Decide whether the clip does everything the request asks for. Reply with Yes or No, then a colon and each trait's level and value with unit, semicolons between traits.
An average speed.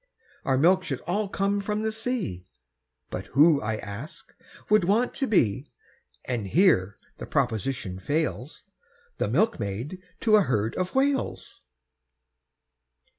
No: slow, 125 wpm